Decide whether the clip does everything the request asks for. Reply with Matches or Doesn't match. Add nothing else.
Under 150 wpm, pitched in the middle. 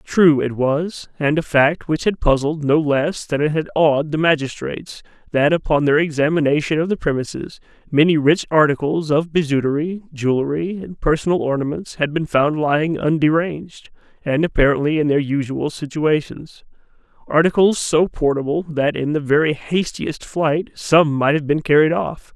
Doesn't match